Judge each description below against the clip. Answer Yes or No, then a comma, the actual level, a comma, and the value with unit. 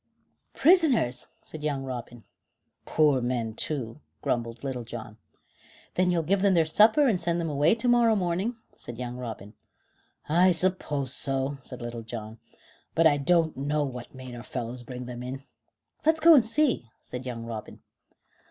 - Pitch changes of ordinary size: No, wide, 6.7 semitones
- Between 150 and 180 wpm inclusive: Yes, average, 160 wpm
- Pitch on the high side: No, medium, 140 Hz